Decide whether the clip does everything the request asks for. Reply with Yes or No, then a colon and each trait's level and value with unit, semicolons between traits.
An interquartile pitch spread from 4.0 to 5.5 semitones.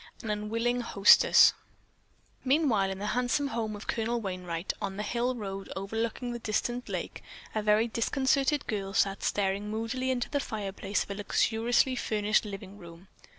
No: average, 3.4 semitones